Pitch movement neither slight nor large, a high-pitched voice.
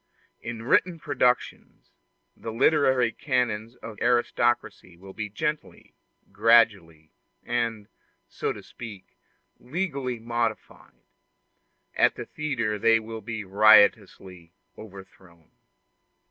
No: average, 3.2 semitones; low, 115 Hz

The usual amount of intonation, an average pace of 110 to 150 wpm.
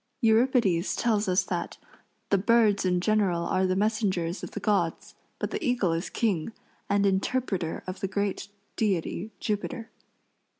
Yes: average, 3.0 semitones; average, 145 wpm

